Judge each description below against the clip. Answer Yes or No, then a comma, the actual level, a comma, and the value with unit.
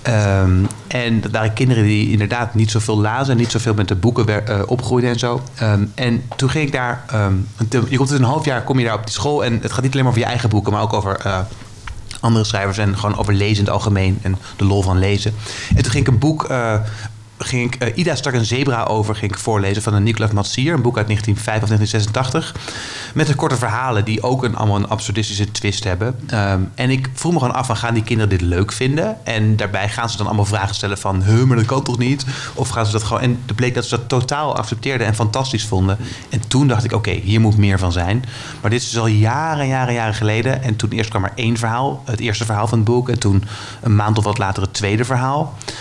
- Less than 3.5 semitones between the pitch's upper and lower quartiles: Yes, average, 3.1 semitones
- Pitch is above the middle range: No, low, 110 Hz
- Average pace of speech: No, fast, 255 wpm